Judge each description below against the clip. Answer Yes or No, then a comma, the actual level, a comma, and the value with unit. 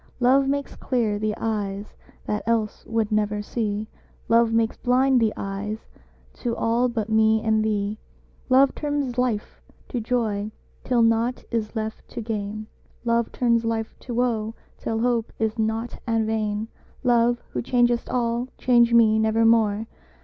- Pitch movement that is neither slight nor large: No, narrow, 1.9 semitones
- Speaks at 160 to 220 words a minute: No, average, 150 wpm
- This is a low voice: No, high, 225 Hz